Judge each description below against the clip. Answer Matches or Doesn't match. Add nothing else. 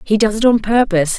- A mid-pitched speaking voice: Doesn't match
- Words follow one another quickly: Matches